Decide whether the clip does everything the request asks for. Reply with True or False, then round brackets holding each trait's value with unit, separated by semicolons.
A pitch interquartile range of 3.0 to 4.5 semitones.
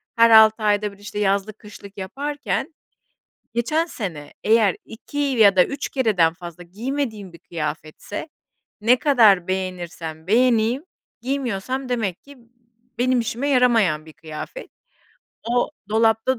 False (5.0 semitones)